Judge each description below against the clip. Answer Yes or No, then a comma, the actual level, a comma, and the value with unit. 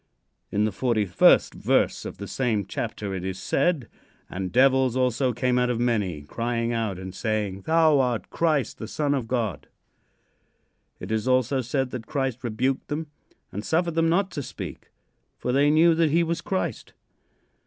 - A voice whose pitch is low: Yes, low, 125 Hz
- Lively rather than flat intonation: No, average, 4.9 semitones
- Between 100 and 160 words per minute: No, average, 175 wpm